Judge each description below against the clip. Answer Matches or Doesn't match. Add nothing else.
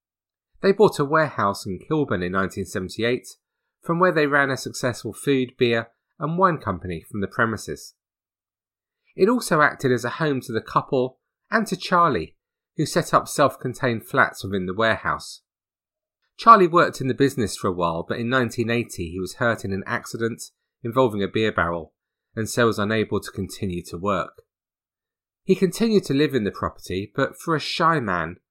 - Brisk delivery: Doesn't match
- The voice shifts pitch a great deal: Matches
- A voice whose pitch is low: Matches